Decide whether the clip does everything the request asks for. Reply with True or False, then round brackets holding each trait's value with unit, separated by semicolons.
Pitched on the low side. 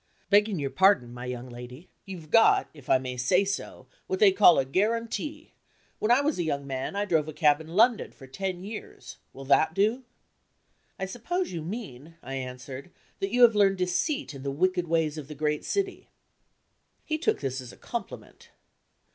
False (175 Hz)